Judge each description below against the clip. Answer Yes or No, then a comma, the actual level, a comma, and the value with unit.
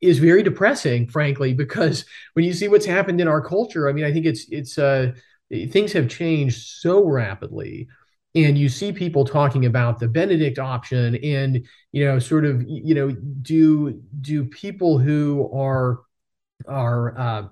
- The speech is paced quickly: No, average, 165 wpm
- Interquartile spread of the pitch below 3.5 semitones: No, average, 3.9 semitones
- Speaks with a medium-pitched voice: Yes, medium, 145 Hz